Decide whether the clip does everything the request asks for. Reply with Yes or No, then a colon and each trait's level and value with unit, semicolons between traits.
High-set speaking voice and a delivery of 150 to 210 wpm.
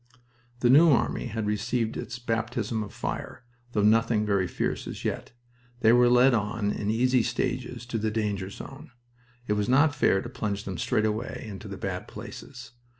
No: low, 115 Hz; average, 180 wpm